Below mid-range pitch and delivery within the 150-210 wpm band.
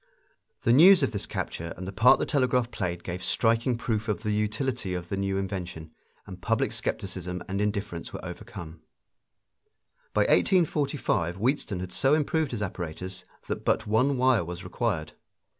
Yes: low, 105 Hz; average, 160 wpm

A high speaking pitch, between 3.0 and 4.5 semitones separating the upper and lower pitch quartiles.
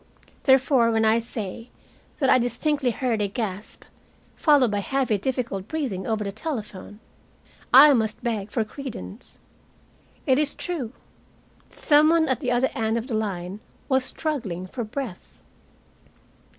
Yes: high, 235 Hz; average, 4.2 semitones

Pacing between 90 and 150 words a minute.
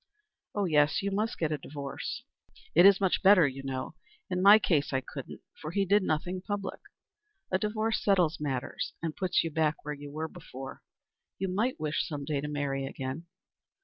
No: average, 185 wpm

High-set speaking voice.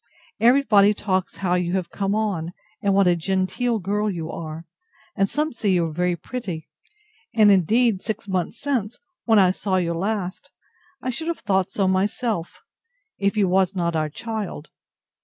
Yes: high, 195 Hz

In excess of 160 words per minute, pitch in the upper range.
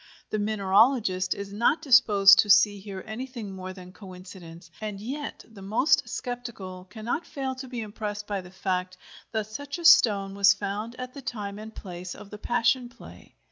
Yes: average, 180 wpm; high, 210 Hz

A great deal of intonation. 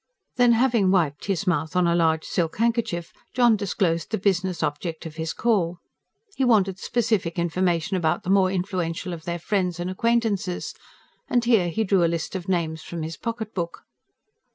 No: average, 4.0 semitones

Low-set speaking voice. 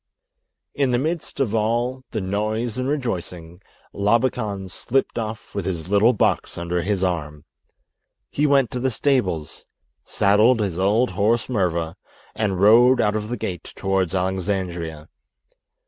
Yes: low, 105 Hz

